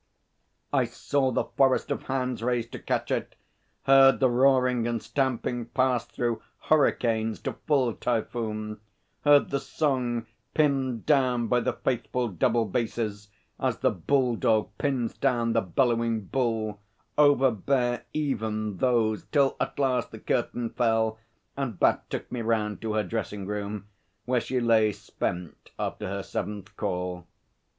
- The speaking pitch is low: Yes, low, 120 Hz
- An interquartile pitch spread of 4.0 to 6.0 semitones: No, average, 3.2 semitones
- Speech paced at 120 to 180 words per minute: Yes, average, 145 wpm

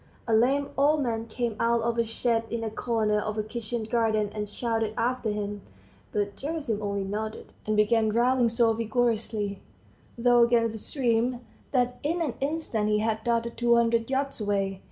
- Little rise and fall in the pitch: Yes, narrow, 2.1 semitones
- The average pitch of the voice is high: Yes, high, 230 Hz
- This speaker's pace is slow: No, average, 175 wpm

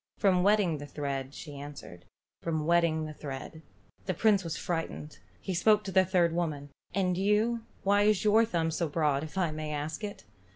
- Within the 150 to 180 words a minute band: No, average, 195 wpm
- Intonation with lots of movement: No, average, 4.3 semitones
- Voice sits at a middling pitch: Yes, medium, 170 Hz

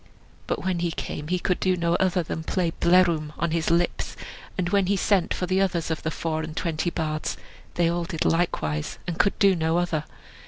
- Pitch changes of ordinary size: No, narrow, 2.1 semitones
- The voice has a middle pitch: Yes, medium, 170 Hz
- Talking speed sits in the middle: No, fast, 210 wpm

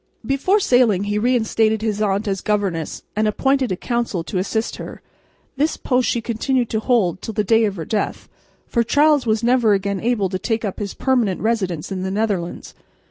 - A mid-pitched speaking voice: No, high, 220 Hz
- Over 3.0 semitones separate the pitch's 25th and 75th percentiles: Yes, average, 3.4 semitones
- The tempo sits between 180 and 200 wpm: Yes, average, 190 wpm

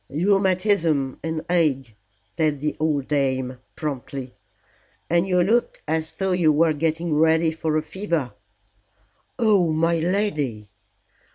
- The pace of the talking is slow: Yes, slow, 120 wpm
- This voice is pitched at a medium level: Yes, medium, 160 Hz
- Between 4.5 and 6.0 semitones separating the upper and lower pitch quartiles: No, average, 3.3 semitones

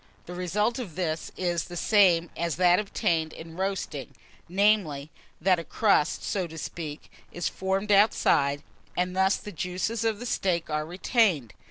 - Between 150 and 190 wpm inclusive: Yes, average, 160 wpm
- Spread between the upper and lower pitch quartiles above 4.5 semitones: No, average, 3.5 semitones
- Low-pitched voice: No, medium, 180 Hz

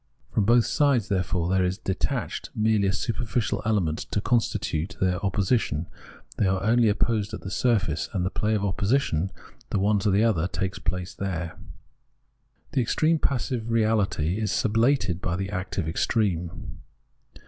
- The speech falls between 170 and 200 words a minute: No, average, 160 wpm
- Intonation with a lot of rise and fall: No, average, 3.5 semitones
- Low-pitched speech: Yes, low, 100 Hz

